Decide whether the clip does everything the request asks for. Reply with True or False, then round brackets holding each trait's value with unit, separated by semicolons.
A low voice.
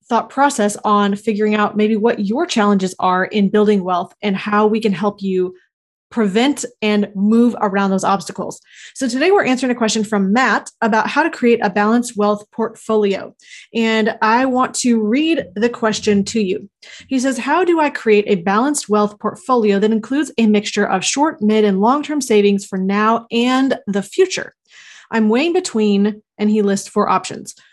False (215 Hz)